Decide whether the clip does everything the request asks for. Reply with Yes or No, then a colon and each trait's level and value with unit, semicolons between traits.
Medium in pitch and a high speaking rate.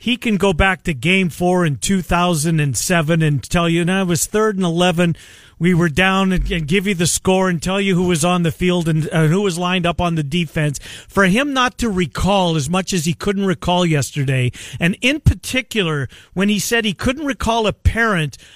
Yes: medium, 180 Hz; fast, 215 wpm